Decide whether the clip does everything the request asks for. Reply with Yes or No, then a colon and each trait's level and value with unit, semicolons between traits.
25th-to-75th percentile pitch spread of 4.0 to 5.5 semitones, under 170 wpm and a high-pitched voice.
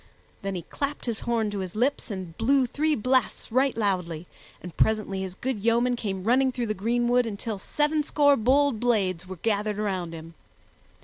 No: average, 4.8 semitones; average, 175 wpm; high, 220 Hz